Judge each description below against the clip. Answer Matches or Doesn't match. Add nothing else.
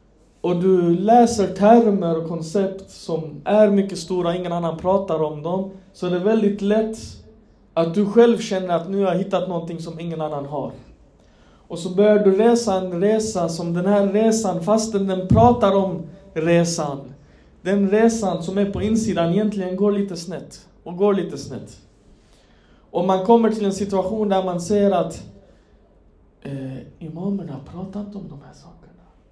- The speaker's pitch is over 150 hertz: Matches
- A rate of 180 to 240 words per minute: Doesn't match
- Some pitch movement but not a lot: Matches